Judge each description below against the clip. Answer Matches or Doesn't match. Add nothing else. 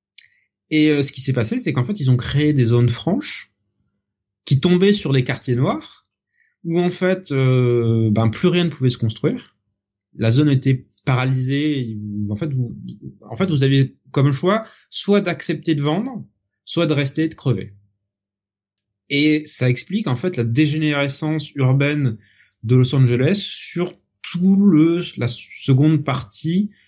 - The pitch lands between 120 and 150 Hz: Matches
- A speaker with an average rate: Matches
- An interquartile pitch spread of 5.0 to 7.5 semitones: Matches